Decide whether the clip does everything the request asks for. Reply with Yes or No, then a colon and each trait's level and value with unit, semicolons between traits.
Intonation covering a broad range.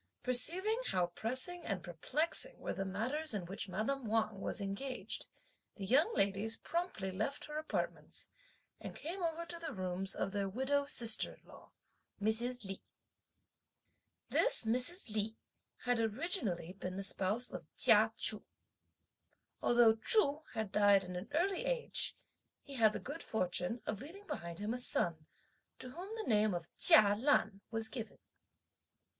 Yes: wide, 6.7 semitones